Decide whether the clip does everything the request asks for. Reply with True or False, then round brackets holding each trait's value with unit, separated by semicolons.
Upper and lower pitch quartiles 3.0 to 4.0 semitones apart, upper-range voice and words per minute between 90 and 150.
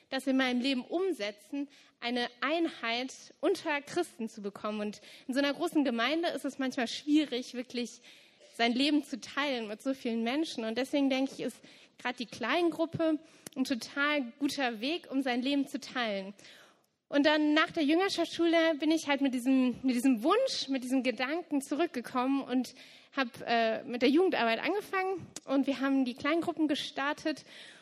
False (3.7 semitones; 275 Hz; 170 wpm)